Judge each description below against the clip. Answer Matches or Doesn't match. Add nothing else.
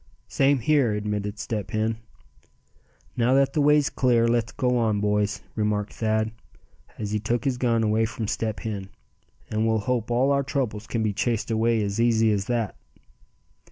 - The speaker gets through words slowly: Doesn't match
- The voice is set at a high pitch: Doesn't match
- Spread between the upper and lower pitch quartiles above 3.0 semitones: Doesn't match